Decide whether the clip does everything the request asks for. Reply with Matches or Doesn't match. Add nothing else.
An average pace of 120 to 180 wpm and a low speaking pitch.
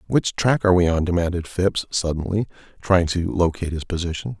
Matches